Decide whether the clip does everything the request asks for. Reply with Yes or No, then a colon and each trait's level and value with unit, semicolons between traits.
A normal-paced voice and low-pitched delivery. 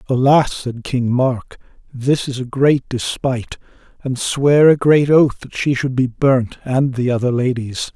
Yes: average, 175 wpm; low, 130 Hz